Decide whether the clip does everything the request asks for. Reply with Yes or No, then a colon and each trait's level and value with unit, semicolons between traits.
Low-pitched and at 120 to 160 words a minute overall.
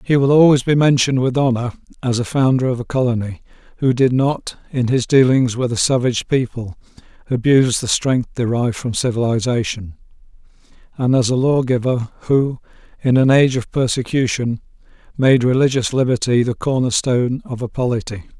Yes: low, 125 Hz; average, 155 wpm